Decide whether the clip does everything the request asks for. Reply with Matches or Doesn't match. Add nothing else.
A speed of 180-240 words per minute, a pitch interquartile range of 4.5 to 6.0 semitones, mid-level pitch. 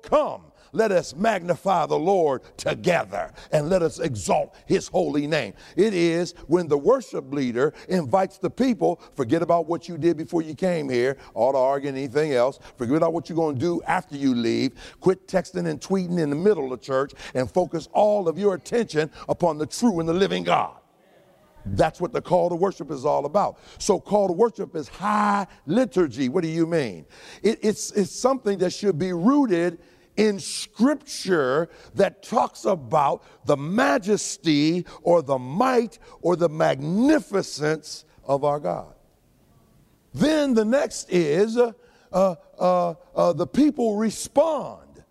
Doesn't match